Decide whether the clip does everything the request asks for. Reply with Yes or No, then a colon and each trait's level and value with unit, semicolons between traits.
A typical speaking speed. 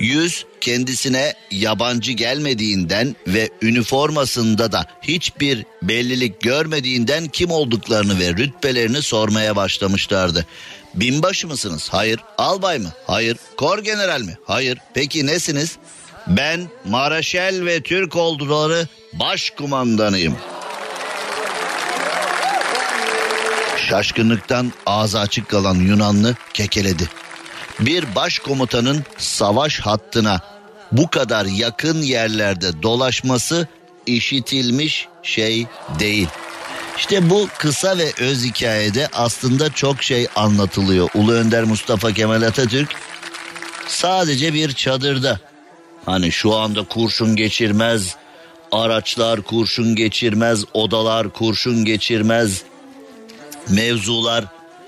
No: slow, 90 wpm